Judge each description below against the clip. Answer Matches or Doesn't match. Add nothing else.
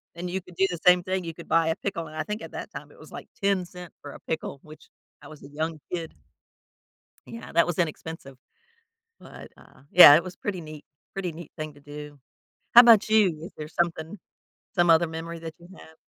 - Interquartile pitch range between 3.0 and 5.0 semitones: Doesn't match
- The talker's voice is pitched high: Doesn't match